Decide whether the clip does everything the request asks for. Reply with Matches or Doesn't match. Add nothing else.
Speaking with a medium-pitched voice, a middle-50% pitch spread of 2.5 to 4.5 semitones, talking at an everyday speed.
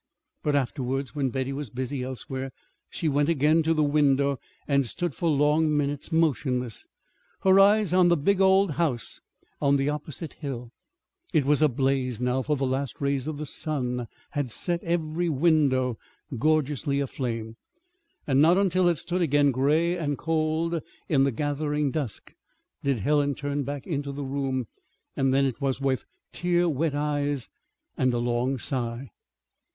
Matches